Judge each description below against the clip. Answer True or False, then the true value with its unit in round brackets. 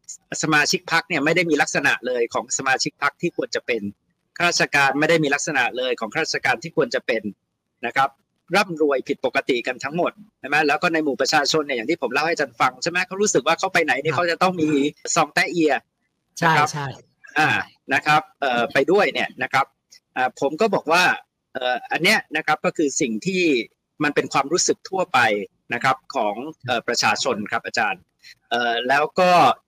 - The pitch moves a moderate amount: True (4.2 semitones)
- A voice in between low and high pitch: True (155 Hz)